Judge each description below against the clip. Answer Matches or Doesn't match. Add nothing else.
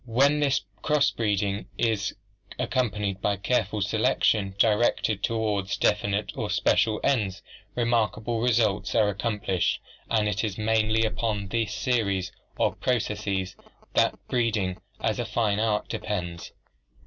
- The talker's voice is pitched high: Doesn't match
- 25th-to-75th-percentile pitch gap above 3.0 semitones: Doesn't match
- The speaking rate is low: Matches